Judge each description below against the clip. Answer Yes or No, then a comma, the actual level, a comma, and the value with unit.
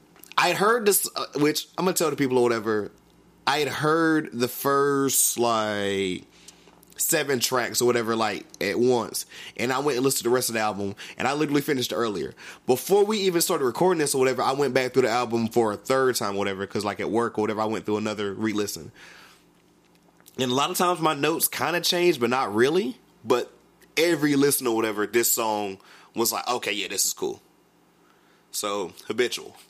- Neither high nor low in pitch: No, low, 125 Hz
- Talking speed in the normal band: No, fast, 210 wpm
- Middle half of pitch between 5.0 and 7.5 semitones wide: Yes, wide, 5.6 semitones